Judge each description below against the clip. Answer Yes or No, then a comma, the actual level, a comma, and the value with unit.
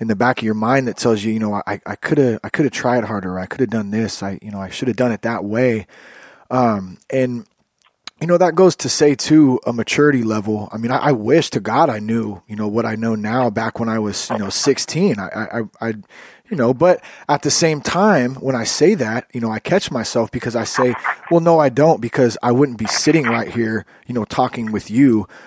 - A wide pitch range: No, average, 3.5 semitones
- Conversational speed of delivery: No, fast, 250 wpm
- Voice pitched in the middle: No, low, 115 Hz